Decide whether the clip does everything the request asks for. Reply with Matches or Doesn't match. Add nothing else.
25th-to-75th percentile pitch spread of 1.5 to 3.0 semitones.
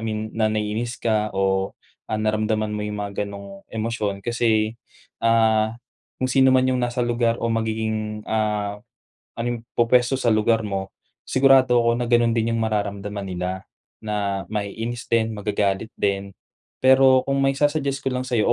Matches